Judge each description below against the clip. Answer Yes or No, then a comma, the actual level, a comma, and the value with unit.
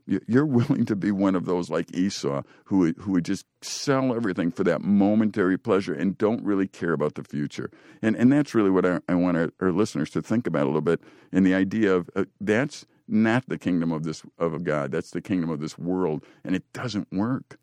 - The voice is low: Yes, very low, 95 Hz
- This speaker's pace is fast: Yes, fast, 230 wpm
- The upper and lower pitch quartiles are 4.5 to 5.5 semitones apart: Yes, average, 4.8 semitones